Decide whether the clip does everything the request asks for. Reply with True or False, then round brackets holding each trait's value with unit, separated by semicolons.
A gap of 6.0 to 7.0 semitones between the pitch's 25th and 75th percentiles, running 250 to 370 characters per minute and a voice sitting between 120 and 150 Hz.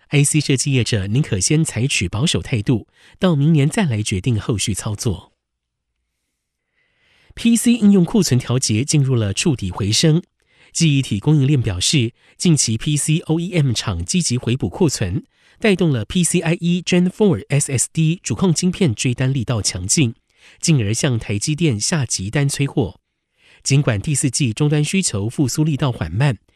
True (6.3 semitones; 260 characters per minute; 140 Hz)